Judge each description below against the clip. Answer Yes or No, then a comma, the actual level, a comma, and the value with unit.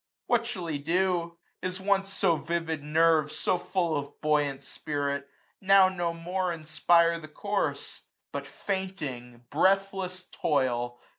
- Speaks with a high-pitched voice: No, medium, 170 Hz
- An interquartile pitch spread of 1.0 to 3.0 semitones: No, average, 4.0 semitones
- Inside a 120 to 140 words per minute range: Yes, slow, 135 wpm